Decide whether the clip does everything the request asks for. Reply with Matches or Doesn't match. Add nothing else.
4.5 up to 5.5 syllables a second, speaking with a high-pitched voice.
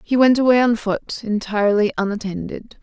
Matches